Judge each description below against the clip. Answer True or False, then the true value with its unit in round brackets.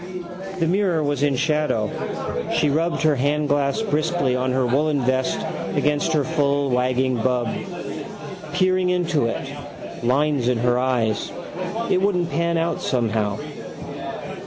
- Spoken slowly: True (130 wpm)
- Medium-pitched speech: True (145 Hz)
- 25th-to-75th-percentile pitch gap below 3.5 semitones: False (4.4 semitones)